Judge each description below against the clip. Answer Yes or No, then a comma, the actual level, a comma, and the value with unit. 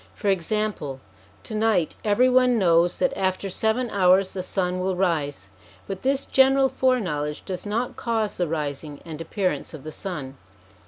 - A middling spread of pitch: Yes, average, 5.0 semitones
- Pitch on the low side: No, high, 190 Hz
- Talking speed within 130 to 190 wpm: Yes, average, 165 wpm